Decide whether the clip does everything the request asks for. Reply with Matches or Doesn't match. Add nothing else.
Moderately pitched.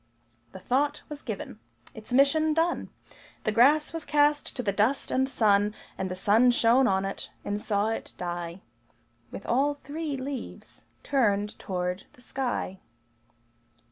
Doesn't match